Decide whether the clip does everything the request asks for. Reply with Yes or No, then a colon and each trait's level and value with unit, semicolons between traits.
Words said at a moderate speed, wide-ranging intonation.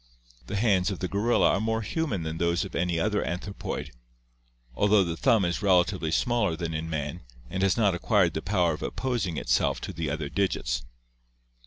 No: average, 185 wpm; average, 4.0 semitones